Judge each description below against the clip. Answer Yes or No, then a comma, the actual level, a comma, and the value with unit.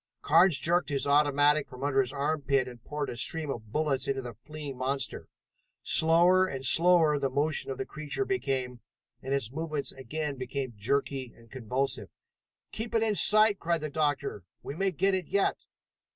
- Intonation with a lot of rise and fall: No, average, 3.4 semitones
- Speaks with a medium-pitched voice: Yes, medium, 145 Hz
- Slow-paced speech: No, average, 175 wpm